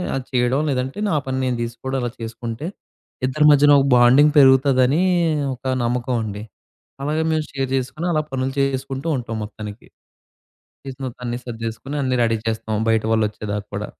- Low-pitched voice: Yes, low, 125 Hz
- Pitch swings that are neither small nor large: Yes, average, 3.0 semitones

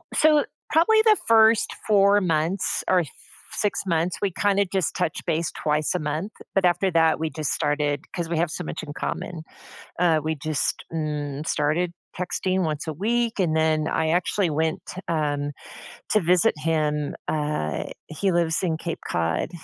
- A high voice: No, medium, 165 Hz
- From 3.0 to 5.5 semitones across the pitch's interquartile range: Yes, average, 3.6 semitones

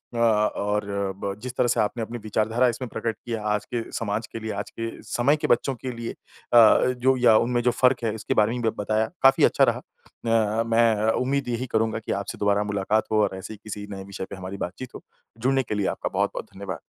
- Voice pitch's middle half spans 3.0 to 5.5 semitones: No, narrow, 2.5 semitones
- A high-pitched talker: No, low, 110 Hz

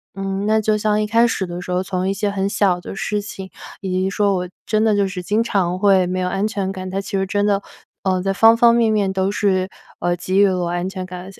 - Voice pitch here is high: Yes, high, 195 Hz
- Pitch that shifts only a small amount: Yes, narrow, 1.9 semitones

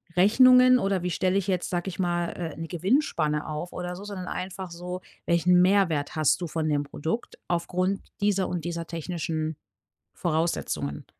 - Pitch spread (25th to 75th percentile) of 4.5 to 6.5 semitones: No, narrow, 2.5 semitones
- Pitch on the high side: No, medium, 175 Hz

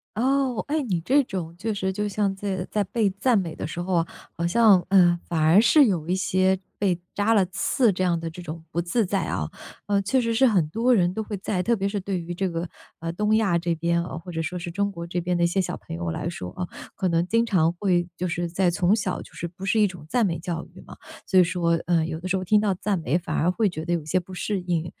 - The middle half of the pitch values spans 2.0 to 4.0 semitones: Yes, average, 3.2 semitones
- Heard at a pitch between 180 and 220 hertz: Yes, medium, 185 Hz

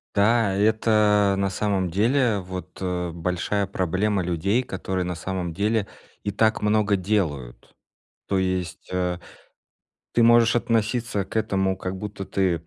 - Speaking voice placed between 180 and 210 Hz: No, low, 100 Hz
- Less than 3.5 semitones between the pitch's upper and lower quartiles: Yes, average, 2.7 semitones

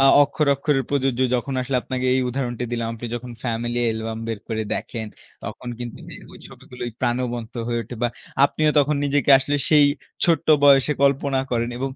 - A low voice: Yes, low, 125 Hz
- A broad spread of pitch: No, average, 2.7 semitones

